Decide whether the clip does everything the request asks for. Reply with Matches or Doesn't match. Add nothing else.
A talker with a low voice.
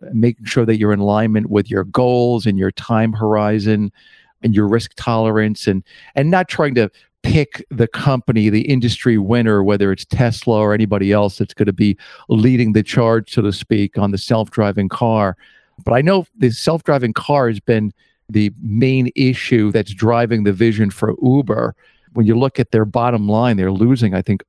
Matches